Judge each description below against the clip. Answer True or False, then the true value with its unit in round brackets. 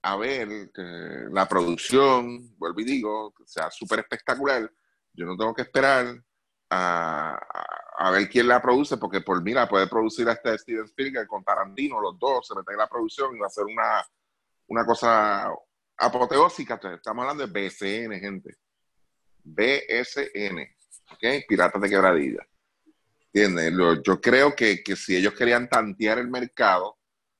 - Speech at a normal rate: True (155 wpm)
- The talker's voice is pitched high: False (120 Hz)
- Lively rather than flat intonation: False (4.2 semitones)